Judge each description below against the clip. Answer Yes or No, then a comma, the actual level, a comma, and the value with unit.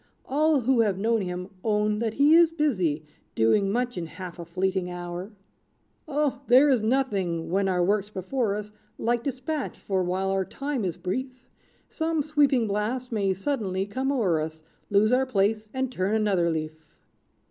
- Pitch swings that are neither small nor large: No, wide, 5.8 semitones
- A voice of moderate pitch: No, high, 210 Hz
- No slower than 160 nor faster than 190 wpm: Yes, average, 170 wpm